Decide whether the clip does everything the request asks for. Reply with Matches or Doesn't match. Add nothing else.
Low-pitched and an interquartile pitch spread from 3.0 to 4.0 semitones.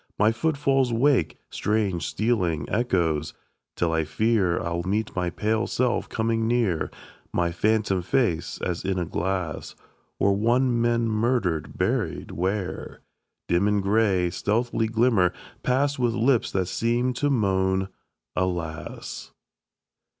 Doesn't match